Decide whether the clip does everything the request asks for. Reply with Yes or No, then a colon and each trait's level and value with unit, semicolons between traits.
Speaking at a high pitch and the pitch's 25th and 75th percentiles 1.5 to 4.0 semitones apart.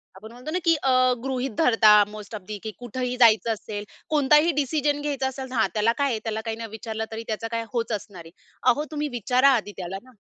Yes: high, 235 Hz; average, 3.5 semitones